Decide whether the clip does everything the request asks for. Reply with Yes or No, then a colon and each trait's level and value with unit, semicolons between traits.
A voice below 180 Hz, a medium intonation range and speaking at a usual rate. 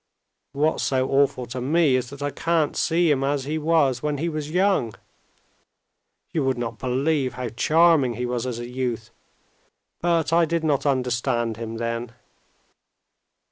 Yes: low, 135 Hz; average, 4.3 semitones; average, 160 wpm